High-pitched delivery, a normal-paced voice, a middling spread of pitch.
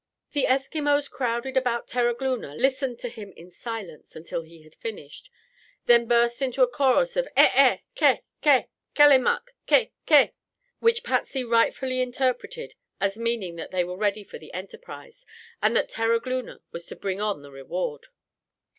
Yes: high, 245 Hz; average, 155 wpm; average, 5.0 semitones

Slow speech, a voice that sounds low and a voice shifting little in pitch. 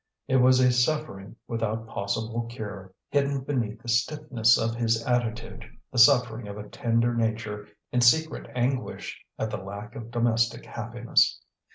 No: average, 150 wpm; low, 115 Hz; narrow, 1.8 semitones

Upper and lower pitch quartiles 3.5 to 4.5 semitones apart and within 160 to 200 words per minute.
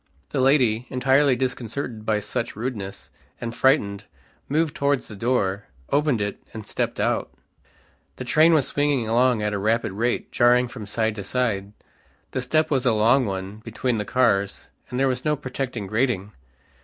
Yes: average, 3.8 semitones; average, 170 wpm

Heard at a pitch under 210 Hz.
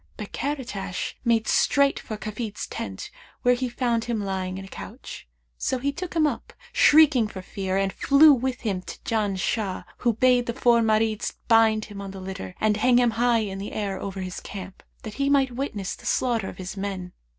No: high, 220 Hz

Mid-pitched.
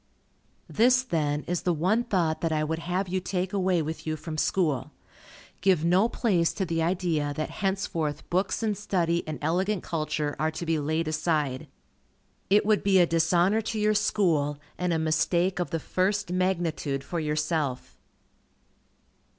Yes: medium, 170 Hz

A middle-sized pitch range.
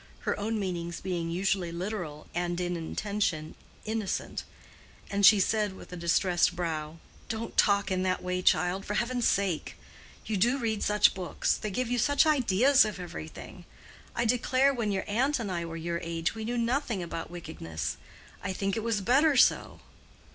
Yes: average, 4.5 semitones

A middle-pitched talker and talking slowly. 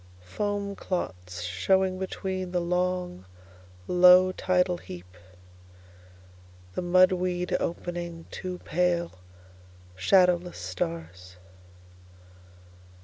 Yes: medium, 175 Hz; slow, 70 wpm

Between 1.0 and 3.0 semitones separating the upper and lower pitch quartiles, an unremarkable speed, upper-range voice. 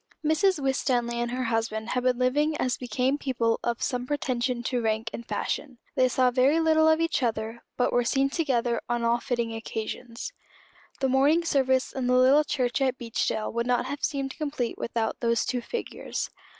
Yes: narrow, 2.6 semitones; average, 185 wpm; very high, 250 Hz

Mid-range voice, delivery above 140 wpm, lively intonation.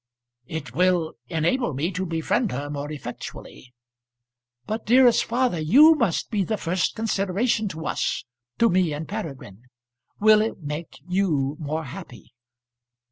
No: medium, 175 Hz; slow, 135 wpm; wide, 6.3 semitones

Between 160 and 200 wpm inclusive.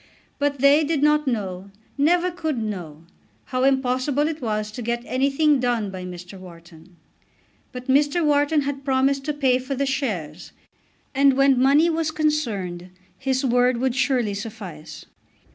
No: average, 150 wpm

